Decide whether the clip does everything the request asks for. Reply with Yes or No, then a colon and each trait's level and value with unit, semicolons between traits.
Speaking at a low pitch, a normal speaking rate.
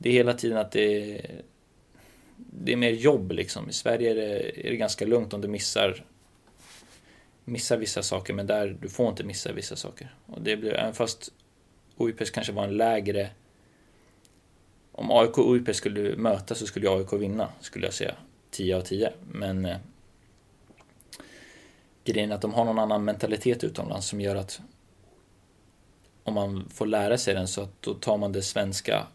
Yes: low, 105 Hz; average, 180 wpm